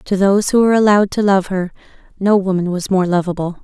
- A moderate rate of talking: No, fast, 215 wpm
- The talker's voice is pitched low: No, high, 190 Hz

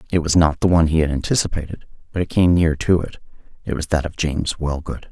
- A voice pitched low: Yes, very low, 80 Hz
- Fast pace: Yes, fast, 235 wpm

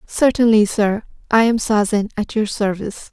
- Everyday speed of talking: Yes, average, 155 wpm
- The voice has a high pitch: Yes, high, 215 Hz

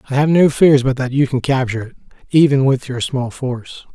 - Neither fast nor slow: No, fast, 230 wpm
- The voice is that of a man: Yes, male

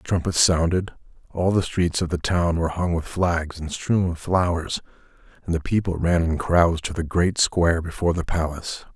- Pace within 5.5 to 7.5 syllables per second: No, 5.1 syllables/s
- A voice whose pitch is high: No, very low, 85 Hz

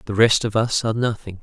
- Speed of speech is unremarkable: No, fast, 250 wpm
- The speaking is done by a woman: No, male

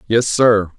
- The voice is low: Yes, low, 110 Hz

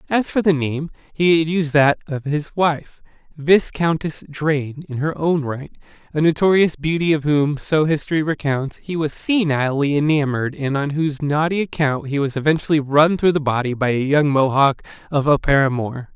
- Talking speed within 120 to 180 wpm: Yes, average, 175 wpm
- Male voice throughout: Yes, male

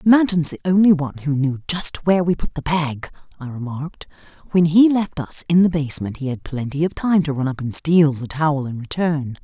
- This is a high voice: No, medium, 155 Hz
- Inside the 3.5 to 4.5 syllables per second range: No, 5.5 syllables/s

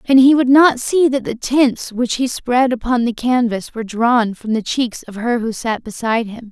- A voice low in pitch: No, high, 240 Hz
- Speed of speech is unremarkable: No, fast, 230 wpm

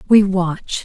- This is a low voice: No, high, 190 Hz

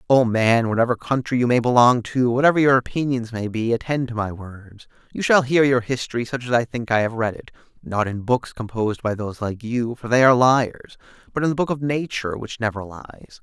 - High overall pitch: No, low, 120 Hz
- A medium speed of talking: No, fast, 230 wpm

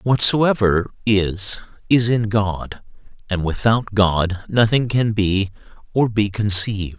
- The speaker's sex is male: Yes, male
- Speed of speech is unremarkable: No, slow, 120 wpm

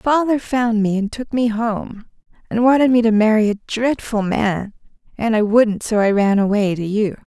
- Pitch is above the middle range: Yes, high, 220 Hz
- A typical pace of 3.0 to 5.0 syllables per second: Yes, 4.6 syllables/s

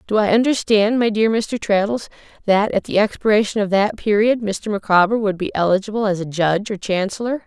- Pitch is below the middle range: No, high, 210 Hz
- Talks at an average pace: Yes, average, 195 wpm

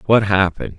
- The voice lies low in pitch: Yes, low, 100 Hz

